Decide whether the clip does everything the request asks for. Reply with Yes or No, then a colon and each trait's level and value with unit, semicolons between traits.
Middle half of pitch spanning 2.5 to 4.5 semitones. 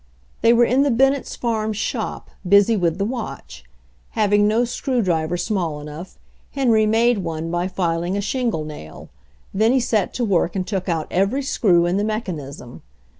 No: average, 5.3 semitones